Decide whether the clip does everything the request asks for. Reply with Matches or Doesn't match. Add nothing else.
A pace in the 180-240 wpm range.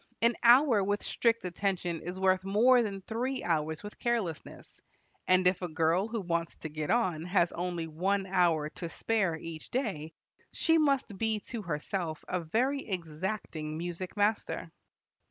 Doesn't match